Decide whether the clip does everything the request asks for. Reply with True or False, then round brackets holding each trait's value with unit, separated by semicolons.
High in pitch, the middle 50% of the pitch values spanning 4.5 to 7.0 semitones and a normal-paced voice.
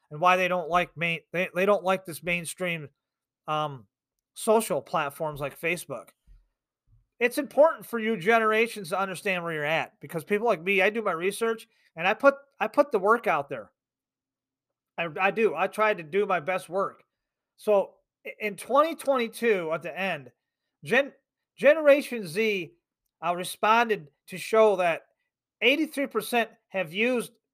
True (195 Hz; 5.1 semitones; 155 wpm)